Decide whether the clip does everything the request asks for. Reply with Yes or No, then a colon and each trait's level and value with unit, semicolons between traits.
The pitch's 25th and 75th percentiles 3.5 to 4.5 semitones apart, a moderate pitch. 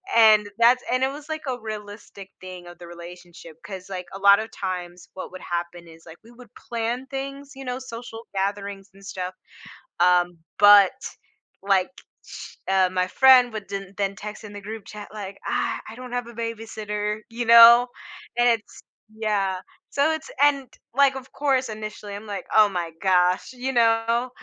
No: average, 4.0 semitones; high, 210 Hz